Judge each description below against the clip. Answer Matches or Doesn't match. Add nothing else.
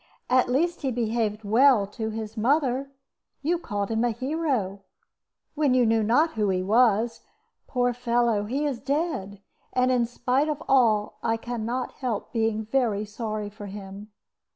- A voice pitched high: Matches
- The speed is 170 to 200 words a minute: Doesn't match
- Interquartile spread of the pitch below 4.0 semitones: Matches